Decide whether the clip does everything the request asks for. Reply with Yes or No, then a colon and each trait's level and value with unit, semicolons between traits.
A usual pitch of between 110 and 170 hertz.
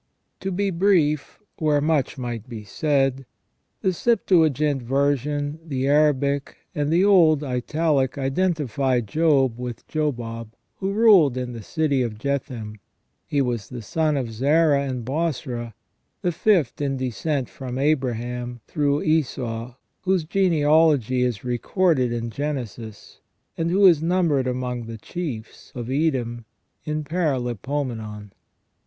Yes: medium, 140 Hz